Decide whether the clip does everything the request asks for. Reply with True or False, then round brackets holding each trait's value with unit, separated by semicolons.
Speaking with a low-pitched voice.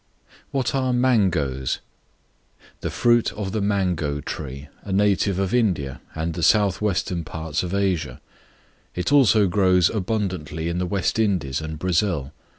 True (90 Hz)